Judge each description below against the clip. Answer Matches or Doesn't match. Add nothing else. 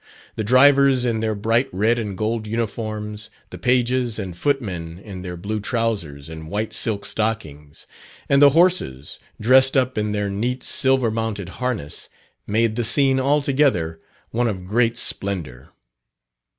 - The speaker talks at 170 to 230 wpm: Doesn't match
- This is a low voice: Matches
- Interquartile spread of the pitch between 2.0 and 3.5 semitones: Doesn't match